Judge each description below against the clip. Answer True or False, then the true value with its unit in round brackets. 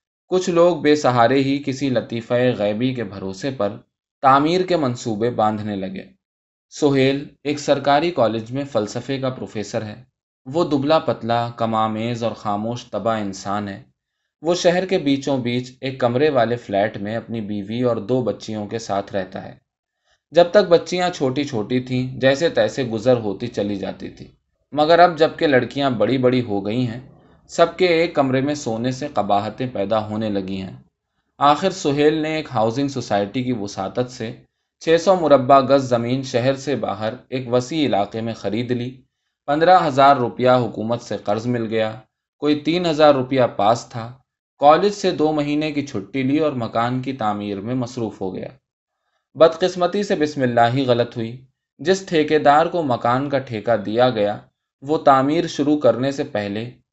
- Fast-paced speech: False (170 wpm)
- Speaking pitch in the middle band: False (125 Hz)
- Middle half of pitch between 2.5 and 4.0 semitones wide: False (4.6 semitones)